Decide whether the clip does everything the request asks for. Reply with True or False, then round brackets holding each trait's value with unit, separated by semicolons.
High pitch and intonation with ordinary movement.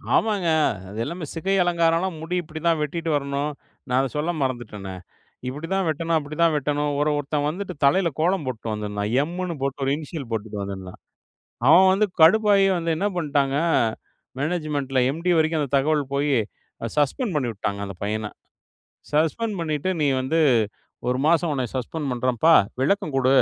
False (150 Hz; 4.0 semitones)